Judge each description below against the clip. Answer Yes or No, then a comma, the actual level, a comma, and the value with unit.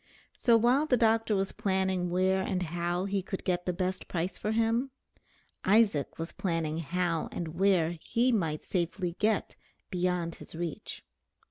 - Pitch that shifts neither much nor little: Yes, average, 3.4 semitones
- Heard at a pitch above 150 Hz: Yes, medium, 185 Hz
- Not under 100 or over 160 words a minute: Yes, average, 155 wpm